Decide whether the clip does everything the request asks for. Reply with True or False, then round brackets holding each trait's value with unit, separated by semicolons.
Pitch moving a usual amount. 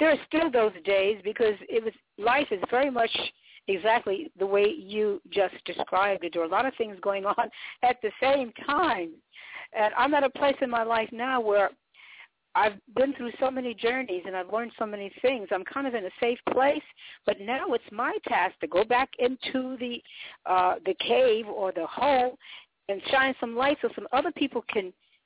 True (4.4 semitones)